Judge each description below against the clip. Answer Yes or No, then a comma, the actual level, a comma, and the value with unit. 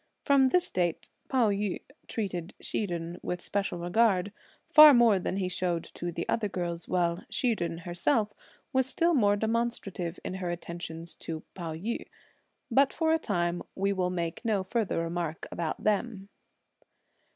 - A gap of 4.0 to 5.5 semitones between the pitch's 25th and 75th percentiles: Yes, average, 4.7 semitones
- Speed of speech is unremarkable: Yes, average, 160 wpm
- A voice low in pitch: No, high, 190 Hz